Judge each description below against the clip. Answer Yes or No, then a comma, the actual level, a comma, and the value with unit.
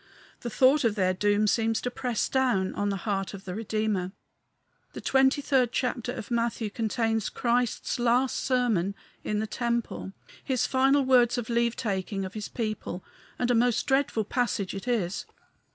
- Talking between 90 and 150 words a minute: No, average, 165 wpm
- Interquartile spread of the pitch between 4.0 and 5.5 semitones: No, average, 3.2 semitones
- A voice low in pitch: No, high, 230 Hz